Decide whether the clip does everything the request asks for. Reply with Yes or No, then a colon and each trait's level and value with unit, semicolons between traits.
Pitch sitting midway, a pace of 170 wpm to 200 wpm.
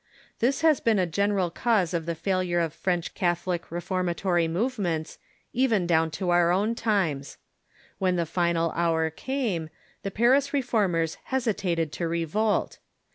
No: medium, 180 Hz; average, 145 wpm